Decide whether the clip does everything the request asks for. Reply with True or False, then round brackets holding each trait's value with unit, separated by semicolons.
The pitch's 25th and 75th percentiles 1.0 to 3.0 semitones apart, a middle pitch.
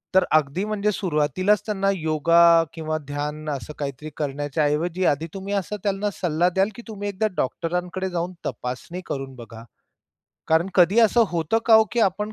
False (4.7 semitones; 170 Hz)